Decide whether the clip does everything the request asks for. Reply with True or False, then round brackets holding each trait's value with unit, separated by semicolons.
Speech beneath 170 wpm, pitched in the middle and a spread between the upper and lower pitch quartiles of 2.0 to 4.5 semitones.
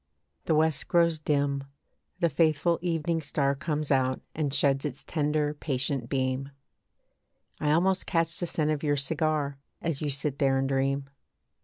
True (155 wpm; 150 Hz; 2.5 semitones)